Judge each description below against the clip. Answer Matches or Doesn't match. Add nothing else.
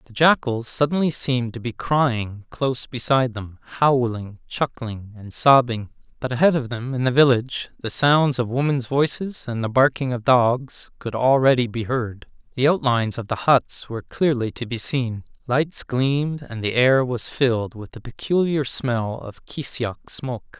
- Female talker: Doesn't match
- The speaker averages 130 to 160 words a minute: Doesn't match